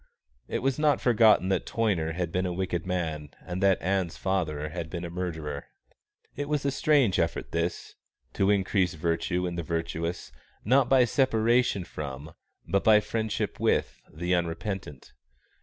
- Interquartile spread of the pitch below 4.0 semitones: No, average, 4.6 semitones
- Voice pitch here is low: Yes, very low, 90 Hz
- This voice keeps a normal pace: Yes, average, 155 wpm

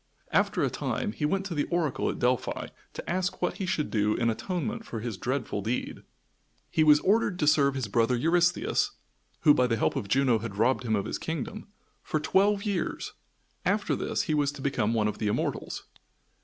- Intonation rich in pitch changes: Yes, wide, 7.1 semitones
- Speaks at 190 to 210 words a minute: Yes, average, 200 wpm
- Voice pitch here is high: No, medium, 140 Hz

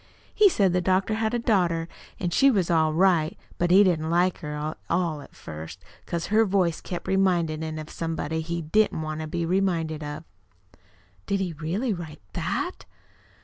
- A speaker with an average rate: Yes, average, 185 wpm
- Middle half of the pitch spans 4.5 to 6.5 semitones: No, average, 3.4 semitones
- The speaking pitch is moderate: Yes, medium, 170 Hz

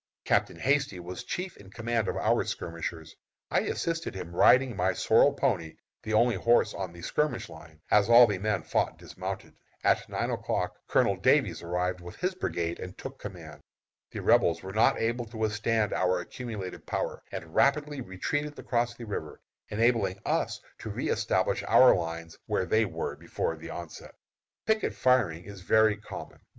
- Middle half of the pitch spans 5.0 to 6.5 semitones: Yes, average, 5.3 semitones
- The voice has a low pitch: Yes, low, 105 Hz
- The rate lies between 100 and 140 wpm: No, average, 165 wpm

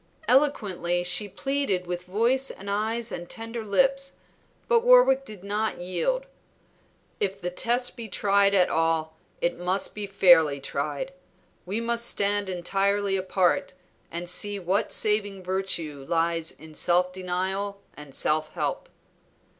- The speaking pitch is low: No, high, 195 Hz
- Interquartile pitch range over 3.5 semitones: Yes, average, 4.0 semitones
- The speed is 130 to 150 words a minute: Yes, slow, 135 wpm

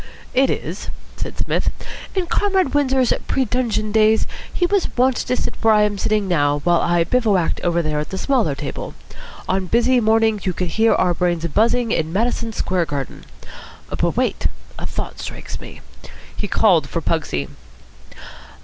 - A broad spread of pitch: Yes, wide, 6.1 semitones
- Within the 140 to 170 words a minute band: Yes, average, 165 wpm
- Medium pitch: No, high, 215 Hz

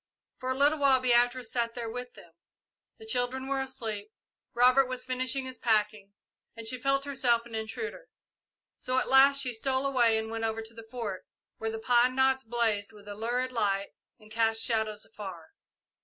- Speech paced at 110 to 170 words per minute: No, average, 185 wpm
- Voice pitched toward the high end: Yes, high, 240 Hz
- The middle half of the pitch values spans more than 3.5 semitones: No, average, 2.8 semitones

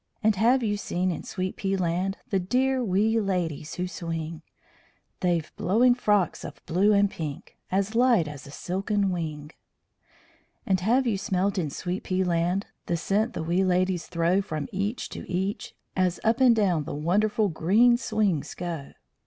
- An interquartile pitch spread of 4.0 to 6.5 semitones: No, average, 3.6 semitones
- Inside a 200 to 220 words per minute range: No, average, 170 wpm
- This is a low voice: No, high, 190 Hz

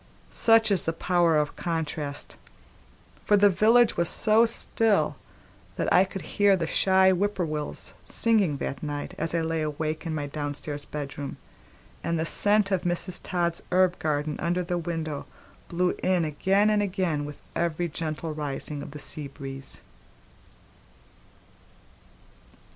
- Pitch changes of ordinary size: Yes, average, 4.0 semitones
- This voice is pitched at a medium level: Yes, medium, 170 Hz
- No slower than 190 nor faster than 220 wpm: No, average, 140 wpm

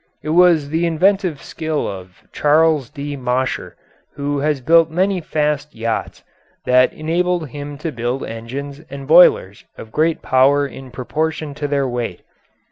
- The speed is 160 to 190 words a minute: No, average, 145 wpm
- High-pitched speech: No, medium, 145 Hz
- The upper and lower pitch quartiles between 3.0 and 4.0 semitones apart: Yes, average, 3.5 semitones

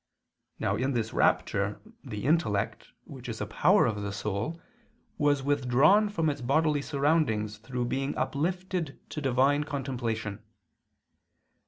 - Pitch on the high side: No, low, 135 Hz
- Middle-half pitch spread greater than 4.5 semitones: Yes, average, 5.2 semitones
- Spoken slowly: Yes, slow, 130 wpm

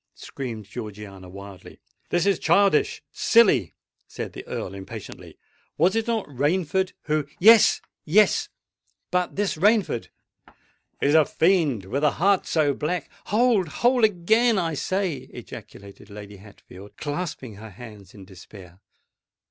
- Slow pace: Yes, slow, 125 wpm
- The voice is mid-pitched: Yes, medium, 150 Hz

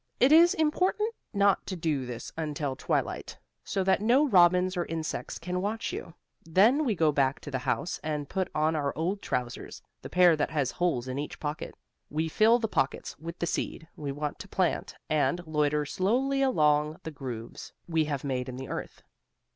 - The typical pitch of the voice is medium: Yes, medium, 160 Hz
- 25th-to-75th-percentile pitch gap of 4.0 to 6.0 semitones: Yes, average, 4.9 semitones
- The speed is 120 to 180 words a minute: No, average, 190 wpm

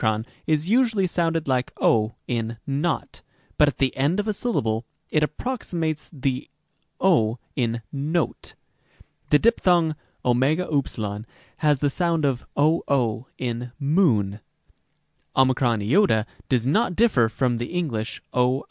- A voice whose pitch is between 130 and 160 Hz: Yes, medium, 140 Hz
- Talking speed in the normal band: No, slow, 130 wpm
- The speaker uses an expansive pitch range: Yes, wide, 5.8 semitones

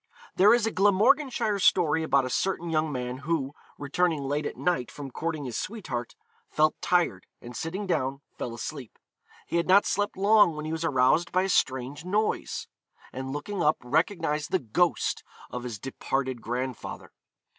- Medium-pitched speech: Yes, medium, 155 Hz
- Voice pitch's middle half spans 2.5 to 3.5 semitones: No, wide, 5.6 semitones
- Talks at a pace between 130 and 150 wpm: No, average, 165 wpm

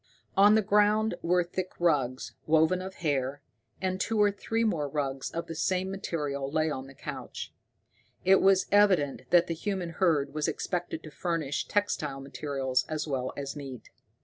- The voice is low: No, medium, 165 Hz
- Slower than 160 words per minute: No, average, 170 wpm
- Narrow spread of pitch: No, average, 5.1 semitones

